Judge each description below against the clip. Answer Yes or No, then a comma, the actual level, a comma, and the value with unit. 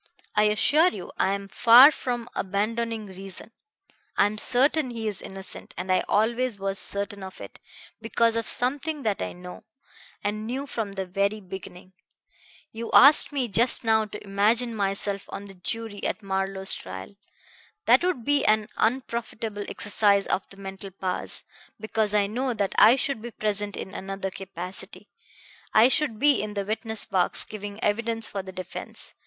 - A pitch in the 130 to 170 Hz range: No, high, 210 Hz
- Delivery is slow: No, average, 165 wpm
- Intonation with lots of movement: No, average, 2.9 semitones